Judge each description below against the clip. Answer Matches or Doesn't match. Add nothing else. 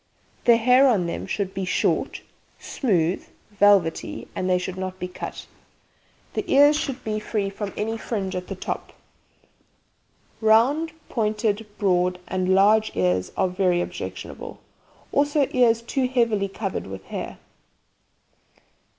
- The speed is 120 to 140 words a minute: Matches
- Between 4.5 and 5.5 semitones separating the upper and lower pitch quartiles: Doesn't match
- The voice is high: Matches